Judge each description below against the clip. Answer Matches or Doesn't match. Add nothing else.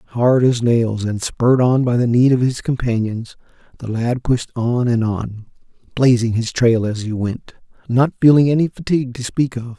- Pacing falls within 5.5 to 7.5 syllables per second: Doesn't match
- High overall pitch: Doesn't match